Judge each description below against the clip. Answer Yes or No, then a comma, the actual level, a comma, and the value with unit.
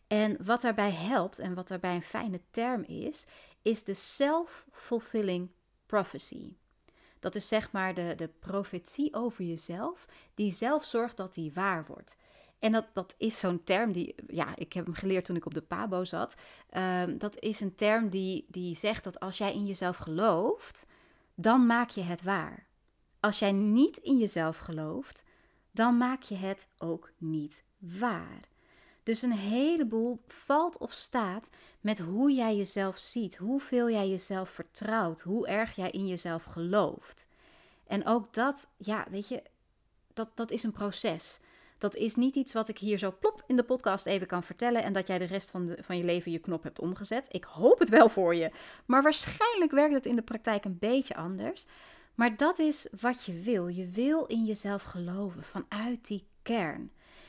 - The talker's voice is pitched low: No, high, 210 Hz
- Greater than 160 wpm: Yes, average, 180 wpm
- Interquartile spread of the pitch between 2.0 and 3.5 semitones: No, average, 4.8 semitones